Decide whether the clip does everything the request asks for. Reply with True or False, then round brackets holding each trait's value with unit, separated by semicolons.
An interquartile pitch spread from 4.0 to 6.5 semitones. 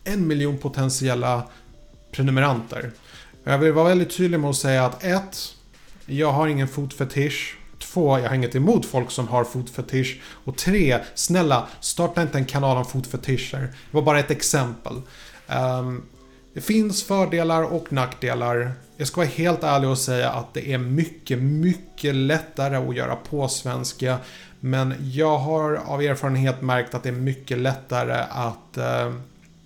False (3.4 semitones)